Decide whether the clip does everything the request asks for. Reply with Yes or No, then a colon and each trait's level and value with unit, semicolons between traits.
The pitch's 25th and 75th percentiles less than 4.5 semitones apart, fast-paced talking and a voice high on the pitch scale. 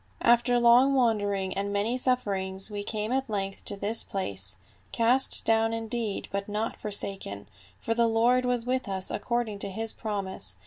No: average, 3.2 semitones; average, 165 wpm; high, 215 Hz